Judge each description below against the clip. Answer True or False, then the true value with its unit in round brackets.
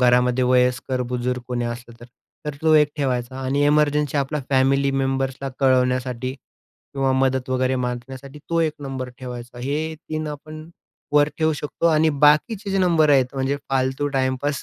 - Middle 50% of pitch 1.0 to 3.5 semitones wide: True (2.7 semitones)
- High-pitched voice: False (135 Hz)